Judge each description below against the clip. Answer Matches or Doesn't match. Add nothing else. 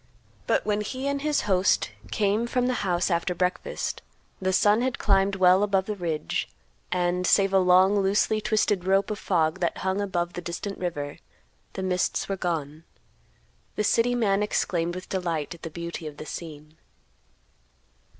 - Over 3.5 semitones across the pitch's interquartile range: Doesn't match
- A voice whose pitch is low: Doesn't match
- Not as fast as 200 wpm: Matches